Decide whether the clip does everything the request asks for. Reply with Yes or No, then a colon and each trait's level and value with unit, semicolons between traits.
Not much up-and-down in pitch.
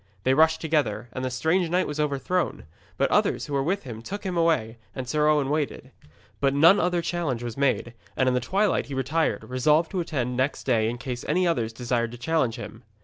No: average, 4.8 semitones